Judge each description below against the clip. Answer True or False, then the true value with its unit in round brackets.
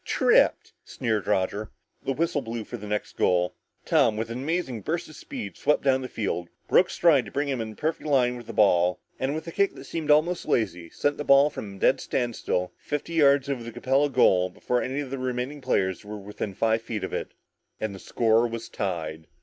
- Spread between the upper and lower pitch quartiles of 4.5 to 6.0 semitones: True (5.3 semitones)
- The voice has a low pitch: True (120 Hz)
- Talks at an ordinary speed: False (215 wpm)